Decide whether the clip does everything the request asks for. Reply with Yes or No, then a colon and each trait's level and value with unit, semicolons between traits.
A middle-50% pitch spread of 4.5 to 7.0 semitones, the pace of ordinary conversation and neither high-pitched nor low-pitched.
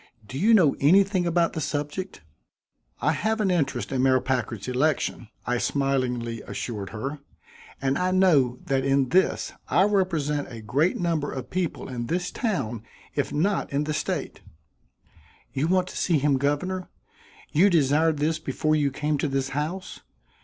Yes: average, 5.0 semitones; average, 160 wpm; medium, 150 Hz